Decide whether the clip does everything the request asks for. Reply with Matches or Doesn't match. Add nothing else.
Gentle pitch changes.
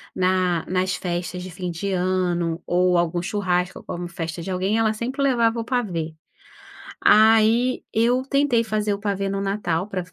Doesn't match